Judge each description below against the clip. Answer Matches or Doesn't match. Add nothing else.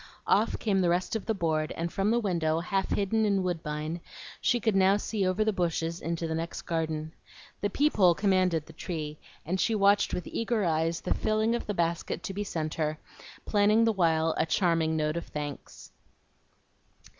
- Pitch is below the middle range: Doesn't match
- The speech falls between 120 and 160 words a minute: Doesn't match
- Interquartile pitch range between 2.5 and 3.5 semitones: Doesn't match